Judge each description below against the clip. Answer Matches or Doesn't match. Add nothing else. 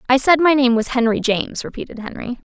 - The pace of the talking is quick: Matches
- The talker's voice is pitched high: Matches